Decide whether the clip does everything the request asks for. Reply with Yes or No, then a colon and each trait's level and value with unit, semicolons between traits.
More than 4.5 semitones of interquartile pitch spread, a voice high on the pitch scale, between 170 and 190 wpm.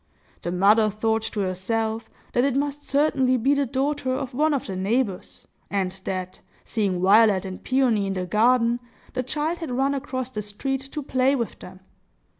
Yes: average, 5.1 semitones; high, 235 Hz; average, 180 wpm